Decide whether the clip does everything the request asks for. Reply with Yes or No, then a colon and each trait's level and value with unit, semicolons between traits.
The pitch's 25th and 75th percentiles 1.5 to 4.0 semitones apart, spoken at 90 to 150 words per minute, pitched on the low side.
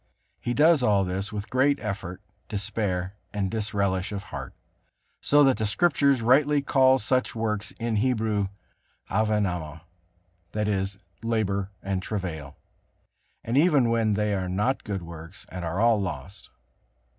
Yes: average, 3.7 semitones; average, 140 wpm; low, 105 Hz